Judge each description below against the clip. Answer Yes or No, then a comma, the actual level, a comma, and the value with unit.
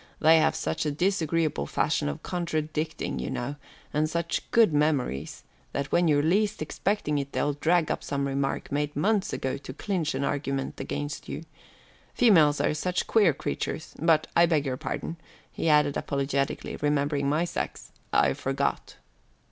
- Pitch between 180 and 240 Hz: No, medium, 150 Hz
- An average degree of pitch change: Yes, average, 3.0 semitones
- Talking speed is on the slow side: No, average, 160 wpm